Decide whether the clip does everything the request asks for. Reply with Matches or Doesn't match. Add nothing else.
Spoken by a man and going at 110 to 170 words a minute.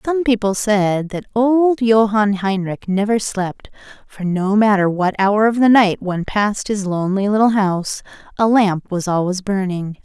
Doesn't match